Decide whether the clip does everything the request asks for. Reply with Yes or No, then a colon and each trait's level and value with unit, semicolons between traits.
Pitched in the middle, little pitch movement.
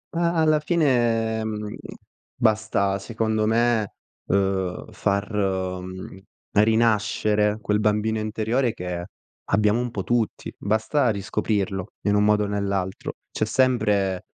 No: low, 105 Hz; narrow, 2.3 semitones